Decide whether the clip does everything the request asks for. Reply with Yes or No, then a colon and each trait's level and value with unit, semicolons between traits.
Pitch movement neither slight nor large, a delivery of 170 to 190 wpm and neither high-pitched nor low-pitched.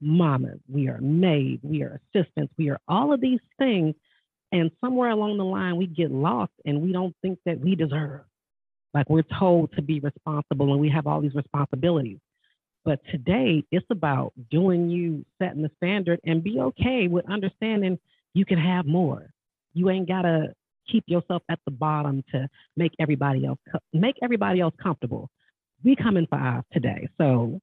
Yes: average, 4.2 semitones; average, 175 wpm; medium, 165 Hz